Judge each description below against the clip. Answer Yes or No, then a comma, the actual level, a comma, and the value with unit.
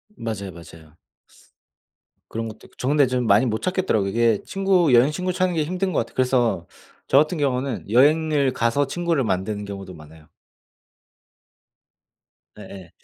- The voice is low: Yes, low, 125 Hz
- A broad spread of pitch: Yes, wide, 7.1 semitones